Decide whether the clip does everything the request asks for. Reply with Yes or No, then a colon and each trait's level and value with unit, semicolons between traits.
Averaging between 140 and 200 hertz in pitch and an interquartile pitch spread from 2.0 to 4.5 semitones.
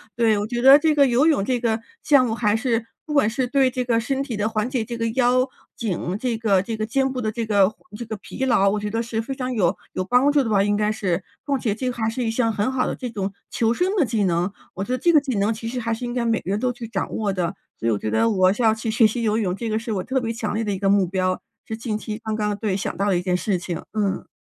No: high, 225 Hz; average, 3.3 semitones